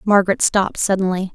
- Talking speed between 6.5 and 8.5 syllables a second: Yes, 6.6 syllables/s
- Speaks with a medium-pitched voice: No, high, 195 Hz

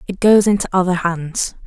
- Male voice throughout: No, female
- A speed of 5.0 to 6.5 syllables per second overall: Yes, 5.1 syllables/s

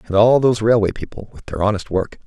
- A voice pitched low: Yes, low, 105 Hz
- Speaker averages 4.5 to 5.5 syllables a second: No, 6.4 syllables/s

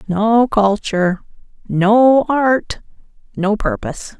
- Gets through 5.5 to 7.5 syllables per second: No, 3.4 syllables/s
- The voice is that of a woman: Yes, female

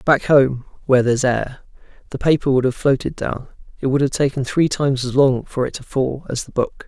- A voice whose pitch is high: No, low, 135 Hz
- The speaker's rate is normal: No, fast, 225 wpm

